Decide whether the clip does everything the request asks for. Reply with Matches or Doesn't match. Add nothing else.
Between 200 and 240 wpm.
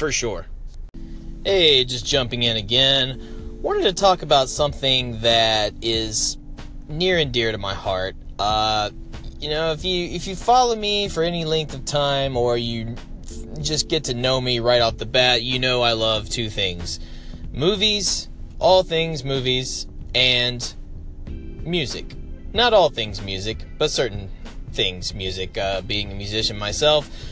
Doesn't match